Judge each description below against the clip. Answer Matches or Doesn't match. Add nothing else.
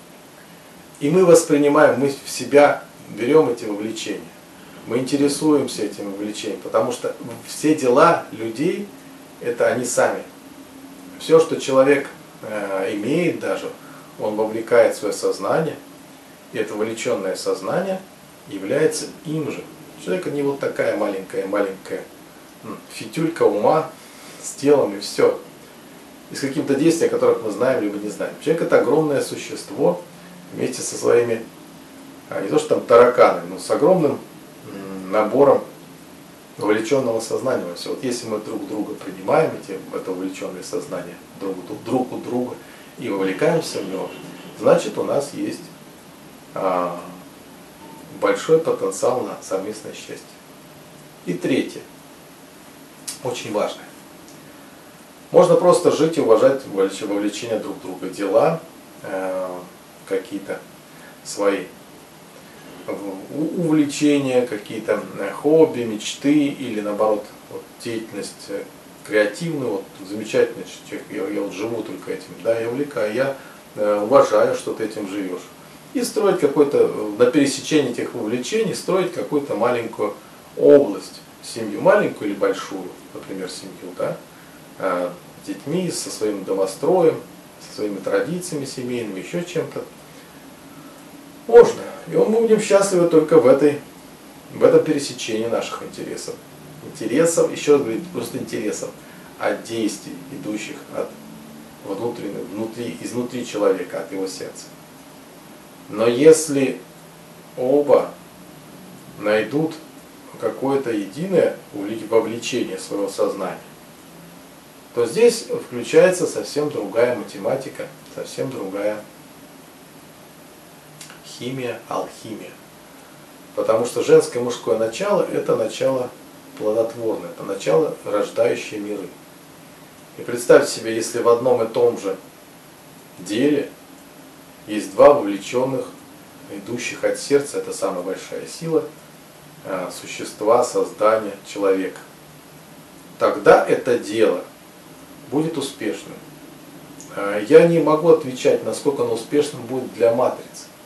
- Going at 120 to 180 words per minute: Doesn't match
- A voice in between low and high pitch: Matches